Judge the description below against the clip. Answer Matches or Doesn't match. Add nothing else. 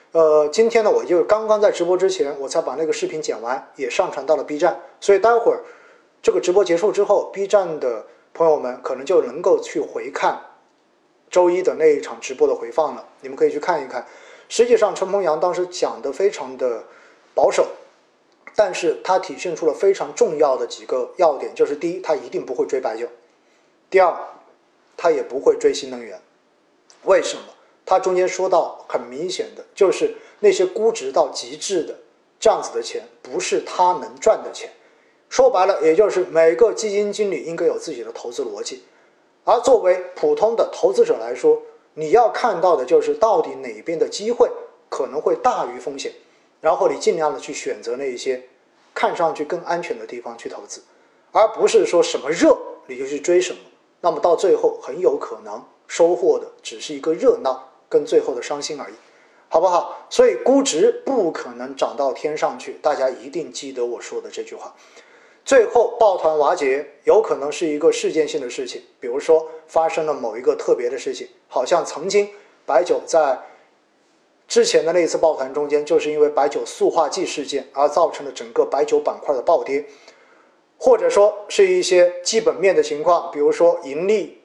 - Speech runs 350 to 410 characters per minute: Doesn't match